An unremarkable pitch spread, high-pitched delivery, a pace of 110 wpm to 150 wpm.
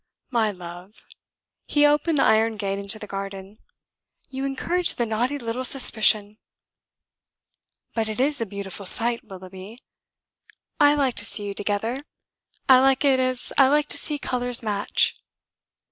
Yes: average, 4.8 semitones; high, 230 Hz; average, 145 wpm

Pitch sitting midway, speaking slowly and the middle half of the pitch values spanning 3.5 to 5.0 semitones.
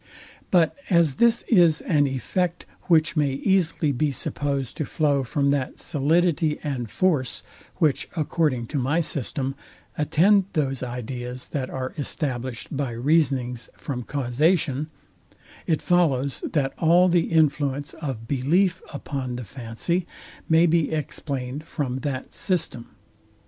Yes: medium, 145 Hz; slow, 130 wpm; average, 3.9 semitones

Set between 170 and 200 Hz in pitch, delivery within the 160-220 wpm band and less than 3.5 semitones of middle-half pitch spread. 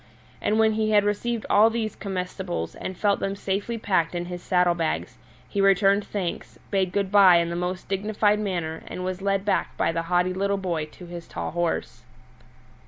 Yes: high, 190 Hz; average, 190 wpm; average, 2.7 semitones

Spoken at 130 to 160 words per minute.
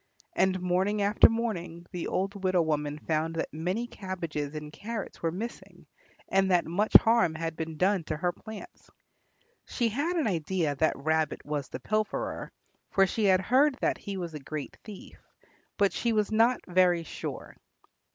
No: average, 170 wpm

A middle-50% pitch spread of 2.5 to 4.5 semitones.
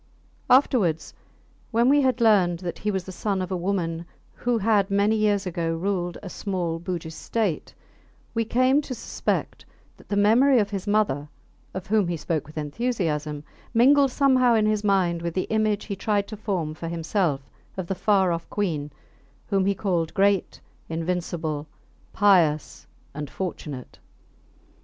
Yes: average, 4.2 semitones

